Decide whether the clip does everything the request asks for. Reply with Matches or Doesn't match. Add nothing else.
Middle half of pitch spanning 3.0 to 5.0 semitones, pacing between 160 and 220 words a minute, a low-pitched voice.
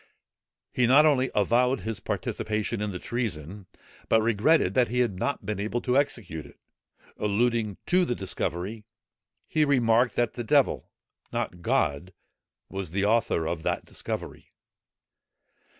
Doesn't match